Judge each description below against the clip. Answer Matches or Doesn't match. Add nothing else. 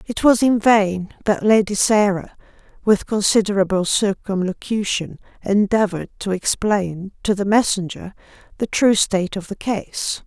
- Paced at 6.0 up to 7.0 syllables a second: Doesn't match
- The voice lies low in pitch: Doesn't match